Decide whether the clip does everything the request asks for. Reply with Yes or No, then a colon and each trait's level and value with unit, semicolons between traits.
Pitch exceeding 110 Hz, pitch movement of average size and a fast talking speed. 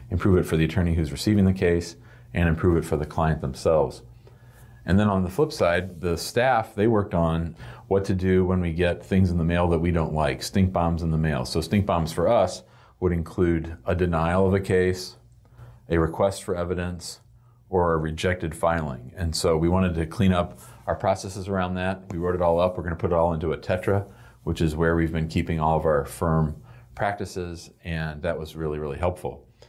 No: very low, 90 Hz; average, 3.0 semitones; fast, 220 wpm